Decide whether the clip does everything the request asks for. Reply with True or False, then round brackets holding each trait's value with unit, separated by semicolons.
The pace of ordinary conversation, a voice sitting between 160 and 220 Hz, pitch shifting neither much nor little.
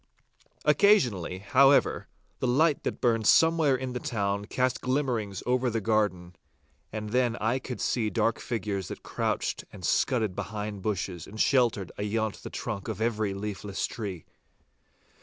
False (145 wpm; 110 Hz; 3.8 semitones)